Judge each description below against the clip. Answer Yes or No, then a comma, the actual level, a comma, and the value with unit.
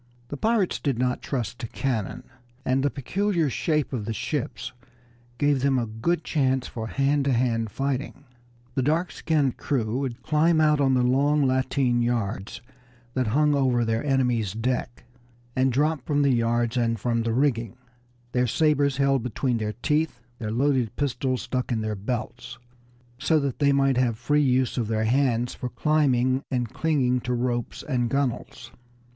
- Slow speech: No, average, 170 wpm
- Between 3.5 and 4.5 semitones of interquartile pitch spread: No, average, 3.0 semitones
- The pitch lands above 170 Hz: No, low, 130 Hz